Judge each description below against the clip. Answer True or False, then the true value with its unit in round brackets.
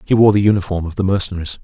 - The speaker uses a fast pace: True (255 wpm)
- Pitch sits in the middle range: False (95 Hz)